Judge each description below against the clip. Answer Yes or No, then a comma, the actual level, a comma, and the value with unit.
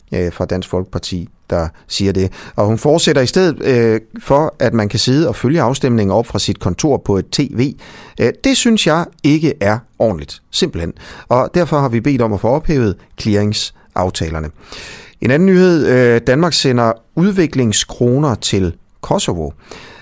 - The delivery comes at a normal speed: Yes, average, 155 wpm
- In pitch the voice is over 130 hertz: No, low, 115 Hz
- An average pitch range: No, wide, 7.1 semitones